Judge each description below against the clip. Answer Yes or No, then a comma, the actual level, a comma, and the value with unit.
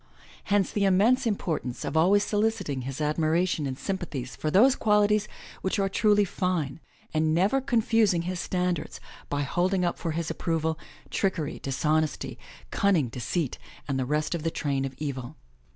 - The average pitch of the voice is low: No, medium, 170 Hz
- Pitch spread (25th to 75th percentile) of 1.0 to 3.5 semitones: No, average, 4.9 semitones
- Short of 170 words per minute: Yes, average, 155 wpm